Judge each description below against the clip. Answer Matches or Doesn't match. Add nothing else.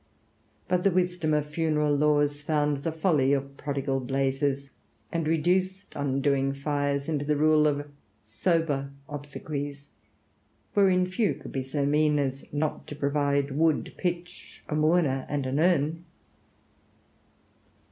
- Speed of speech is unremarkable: Doesn't match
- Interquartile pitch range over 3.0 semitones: Doesn't match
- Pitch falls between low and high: Matches